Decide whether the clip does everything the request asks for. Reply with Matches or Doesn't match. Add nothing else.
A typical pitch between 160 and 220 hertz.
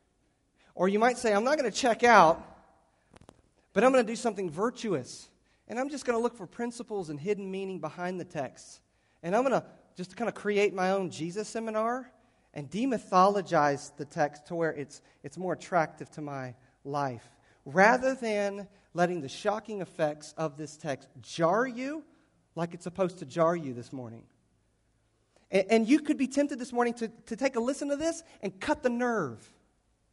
Matches